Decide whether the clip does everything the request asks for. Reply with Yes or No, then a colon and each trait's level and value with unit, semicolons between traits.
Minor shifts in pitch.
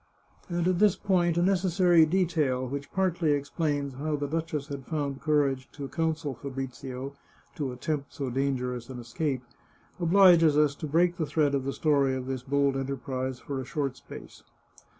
No: average, 3.5 semitones